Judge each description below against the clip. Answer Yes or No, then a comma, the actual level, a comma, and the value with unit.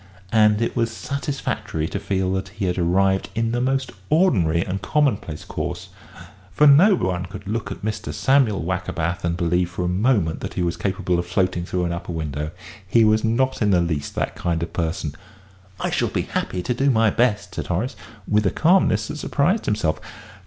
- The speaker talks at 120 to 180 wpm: No, average, 195 wpm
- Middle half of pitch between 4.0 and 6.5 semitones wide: Yes, average, 4.9 semitones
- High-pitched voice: No, very low, 95 Hz